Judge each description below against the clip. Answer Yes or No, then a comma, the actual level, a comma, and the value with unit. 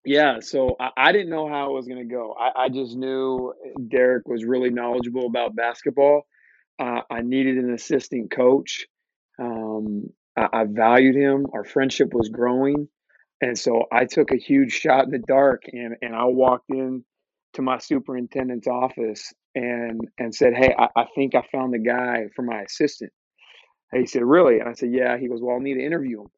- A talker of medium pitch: No, low, 125 Hz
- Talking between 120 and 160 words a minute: No, average, 195 wpm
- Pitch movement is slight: Yes, narrow, 1.8 semitones